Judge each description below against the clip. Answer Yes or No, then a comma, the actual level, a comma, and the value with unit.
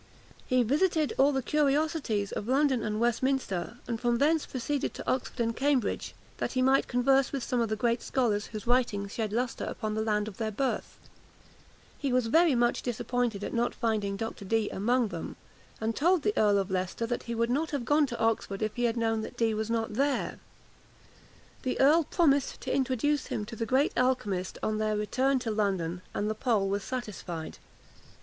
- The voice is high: Yes, high, 235 Hz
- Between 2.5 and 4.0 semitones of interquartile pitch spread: Yes, average, 3.7 semitones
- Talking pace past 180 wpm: Yes, average, 195 wpm